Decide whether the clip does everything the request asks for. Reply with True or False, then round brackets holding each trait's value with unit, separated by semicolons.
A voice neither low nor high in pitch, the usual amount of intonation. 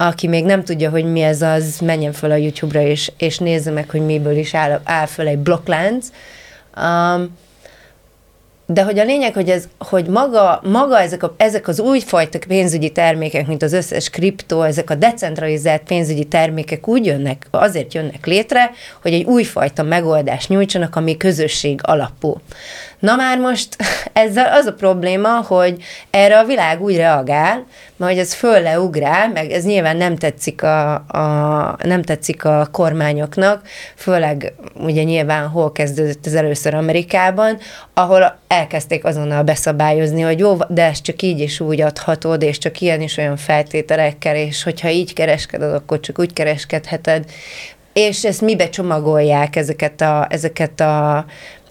True (165 Hz; 3.4 semitones)